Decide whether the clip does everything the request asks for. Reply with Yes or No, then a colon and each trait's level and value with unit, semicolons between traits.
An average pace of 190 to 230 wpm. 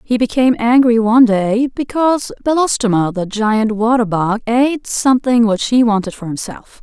No: average, 160 wpm